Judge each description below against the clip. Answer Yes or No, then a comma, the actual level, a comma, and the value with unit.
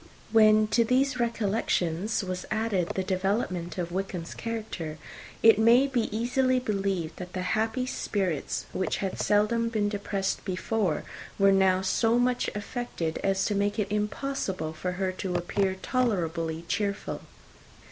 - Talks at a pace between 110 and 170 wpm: Yes, average, 145 wpm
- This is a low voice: No, high, 200 Hz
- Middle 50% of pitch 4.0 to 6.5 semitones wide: No, average, 3.5 semitones